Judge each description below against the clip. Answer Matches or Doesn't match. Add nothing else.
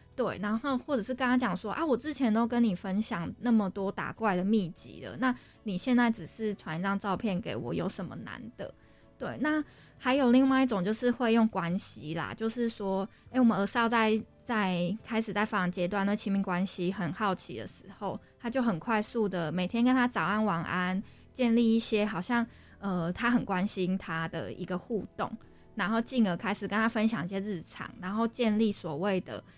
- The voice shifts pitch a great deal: Doesn't match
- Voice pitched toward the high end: Matches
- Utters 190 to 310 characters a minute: Matches